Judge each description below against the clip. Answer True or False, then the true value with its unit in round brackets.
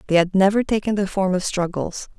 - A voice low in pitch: False (190 Hz)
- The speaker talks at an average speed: False (220 wpm)